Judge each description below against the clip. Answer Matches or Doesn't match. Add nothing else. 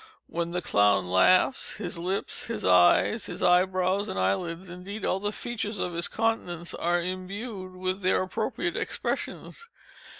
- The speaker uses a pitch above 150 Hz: Matches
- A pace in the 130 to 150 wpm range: Matches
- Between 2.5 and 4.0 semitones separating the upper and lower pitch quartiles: Matches